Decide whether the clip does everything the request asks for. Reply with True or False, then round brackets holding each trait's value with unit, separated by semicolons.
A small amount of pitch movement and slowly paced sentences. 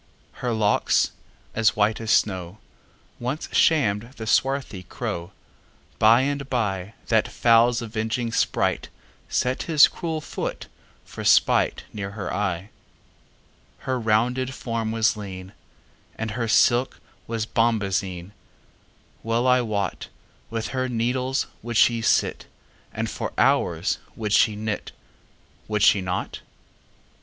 False (3.0 semitones; 95 wpm)